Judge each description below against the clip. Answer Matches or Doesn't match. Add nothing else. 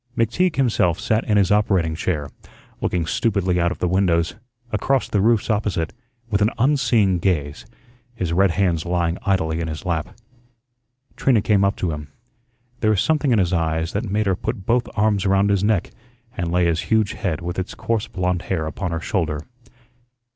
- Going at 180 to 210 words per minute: Matches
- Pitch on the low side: Matches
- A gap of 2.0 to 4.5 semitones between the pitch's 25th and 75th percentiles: Matches